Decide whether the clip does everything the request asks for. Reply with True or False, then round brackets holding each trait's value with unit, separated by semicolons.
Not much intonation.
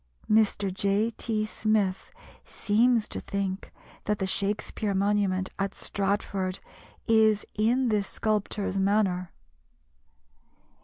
True (1.7 semitones)